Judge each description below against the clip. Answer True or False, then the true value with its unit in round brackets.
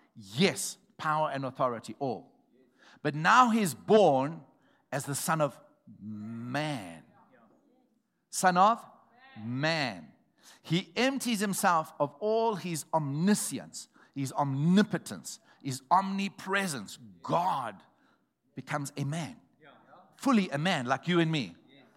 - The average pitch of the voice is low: False (160 Hz)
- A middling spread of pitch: False (6.0 semitones)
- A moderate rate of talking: False (105 wpm)